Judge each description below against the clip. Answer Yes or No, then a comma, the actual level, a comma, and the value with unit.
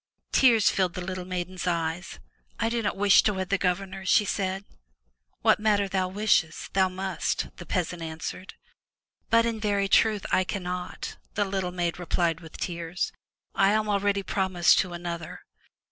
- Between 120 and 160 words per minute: No, average, 175 wpm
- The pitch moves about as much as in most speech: No, narrow, 2.3 semitones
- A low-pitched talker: No, medium, 185 Hz